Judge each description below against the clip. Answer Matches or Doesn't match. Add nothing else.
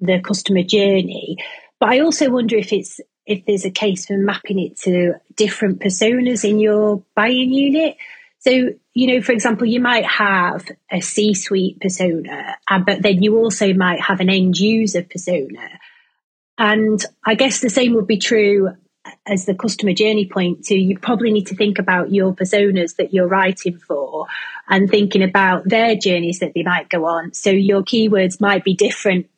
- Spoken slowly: Doesn't match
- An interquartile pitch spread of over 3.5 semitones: Doesn't match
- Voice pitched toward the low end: Doesn't match